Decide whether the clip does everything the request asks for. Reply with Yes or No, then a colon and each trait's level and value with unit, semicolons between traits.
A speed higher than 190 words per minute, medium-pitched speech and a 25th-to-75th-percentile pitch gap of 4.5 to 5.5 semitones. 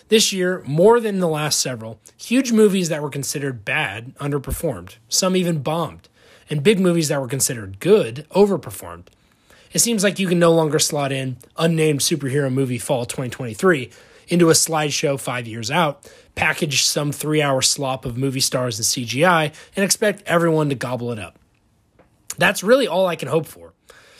No: average, 170 wpm; medium, 150 Hz; average, 4.9 semitones